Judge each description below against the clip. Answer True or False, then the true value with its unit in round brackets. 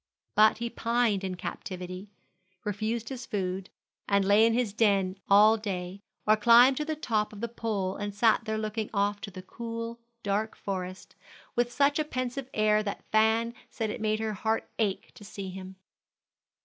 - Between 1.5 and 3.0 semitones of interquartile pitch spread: True (2.6 semitones)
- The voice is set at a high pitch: True (215 Hz)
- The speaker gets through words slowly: False (175 wpm)